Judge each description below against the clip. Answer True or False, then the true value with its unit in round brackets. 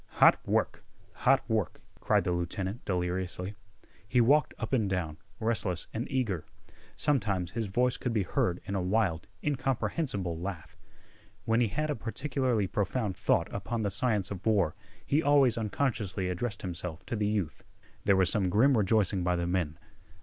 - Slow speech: False (165 wpm)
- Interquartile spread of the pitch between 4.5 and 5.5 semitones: True (4.9 semitones)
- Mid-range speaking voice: False (100 Hz)